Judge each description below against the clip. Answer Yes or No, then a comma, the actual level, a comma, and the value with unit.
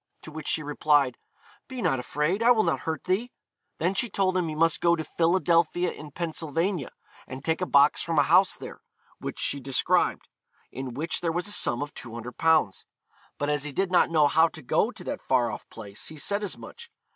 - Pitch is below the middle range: No, medium, 160 Hz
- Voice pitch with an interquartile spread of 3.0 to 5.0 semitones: Yes, average, 3.9 semitones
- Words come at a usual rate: No, fast, 210 wpm